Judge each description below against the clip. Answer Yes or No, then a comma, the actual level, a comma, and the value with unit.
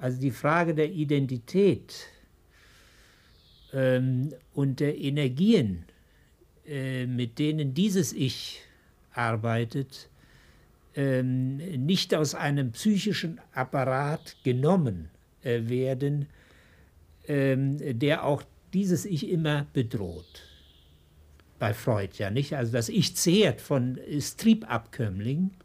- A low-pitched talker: Yes, low, 130 Hz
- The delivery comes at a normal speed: No, slow, 95 wpm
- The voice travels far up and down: Yes, wide, 6.0 semitones